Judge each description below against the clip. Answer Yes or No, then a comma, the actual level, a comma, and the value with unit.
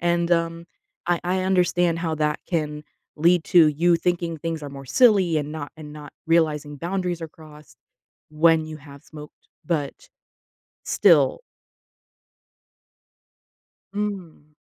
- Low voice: No, medium, 165 Hz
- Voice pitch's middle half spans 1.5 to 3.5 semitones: Yes, narrow, 2.6 semitones